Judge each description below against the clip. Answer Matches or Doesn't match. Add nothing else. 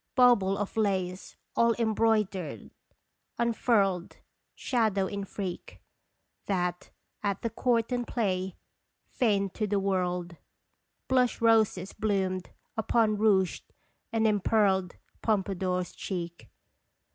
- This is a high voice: Matches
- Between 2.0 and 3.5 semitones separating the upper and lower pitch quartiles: Matches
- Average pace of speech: Doesn't match